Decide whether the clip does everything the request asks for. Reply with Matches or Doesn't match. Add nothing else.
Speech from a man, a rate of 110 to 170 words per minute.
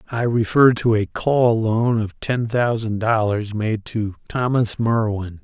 Matches